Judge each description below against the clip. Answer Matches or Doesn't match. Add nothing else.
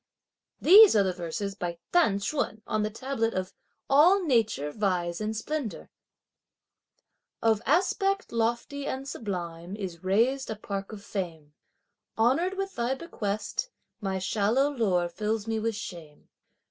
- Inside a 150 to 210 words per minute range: Doesn't match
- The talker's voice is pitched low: Doesn't match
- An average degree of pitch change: Doesn't match